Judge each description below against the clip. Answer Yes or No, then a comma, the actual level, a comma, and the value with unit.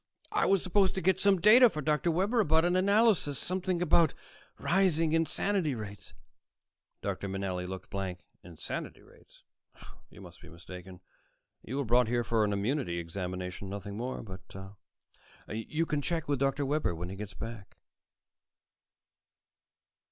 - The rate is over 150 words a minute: No, average, 145 wpm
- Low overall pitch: Yes, low, 130 Hz